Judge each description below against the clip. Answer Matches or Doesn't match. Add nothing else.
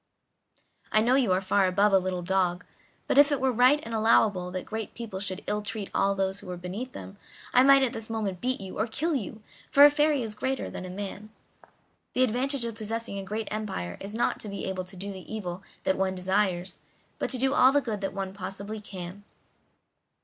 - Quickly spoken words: Matches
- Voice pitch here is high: Matches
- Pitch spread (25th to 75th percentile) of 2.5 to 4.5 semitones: Matches